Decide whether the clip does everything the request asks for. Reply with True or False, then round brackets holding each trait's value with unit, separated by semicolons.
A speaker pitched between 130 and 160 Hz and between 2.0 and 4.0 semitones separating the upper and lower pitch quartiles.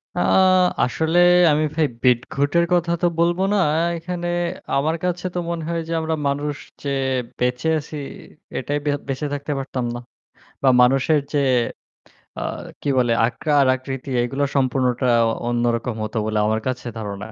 False (140 Hz; 4.5 semitones)